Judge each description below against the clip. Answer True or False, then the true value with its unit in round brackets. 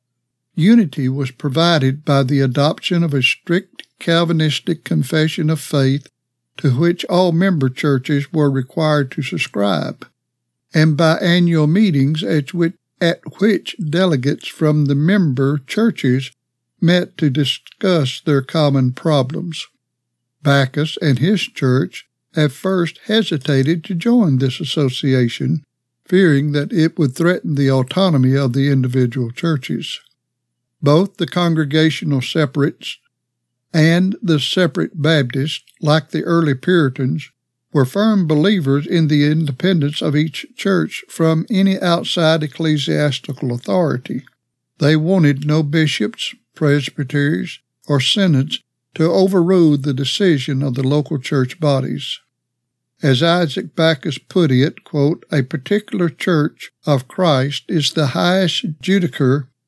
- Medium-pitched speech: True (150 Hz)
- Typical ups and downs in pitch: True (3.8 semitones)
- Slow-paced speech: True (120 wpm)